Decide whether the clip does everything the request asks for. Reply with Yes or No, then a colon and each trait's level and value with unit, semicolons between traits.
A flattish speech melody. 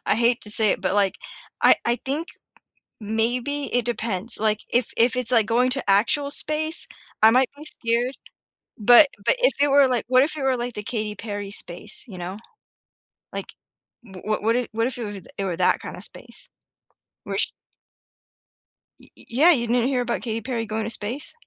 No: average, 3.2 semitones